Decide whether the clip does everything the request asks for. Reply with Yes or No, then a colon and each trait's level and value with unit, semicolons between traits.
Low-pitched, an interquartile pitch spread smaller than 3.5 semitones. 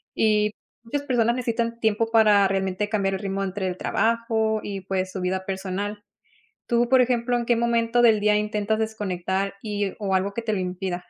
No: high, 210 Hz; average, 3.0 semitones